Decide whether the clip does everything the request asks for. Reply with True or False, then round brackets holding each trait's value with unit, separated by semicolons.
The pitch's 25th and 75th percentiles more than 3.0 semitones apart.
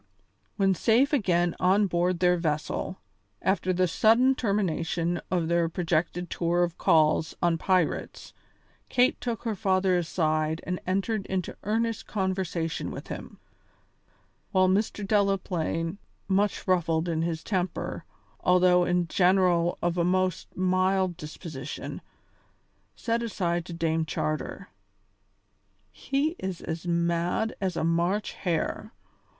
False (2.5 semitones)